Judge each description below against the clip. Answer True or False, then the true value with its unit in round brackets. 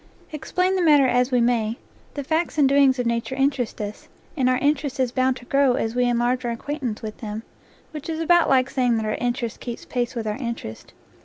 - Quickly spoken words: True (225 wpm)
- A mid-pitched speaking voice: False (255 Hz)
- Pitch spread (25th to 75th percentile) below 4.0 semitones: True (3.1 semitones)